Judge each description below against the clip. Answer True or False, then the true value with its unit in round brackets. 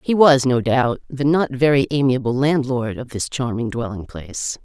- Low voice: True (130 Hz)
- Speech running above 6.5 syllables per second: False (4.8 syllables/s)